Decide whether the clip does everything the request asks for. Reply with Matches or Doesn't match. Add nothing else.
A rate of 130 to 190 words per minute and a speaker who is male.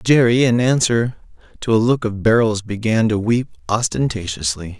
Matches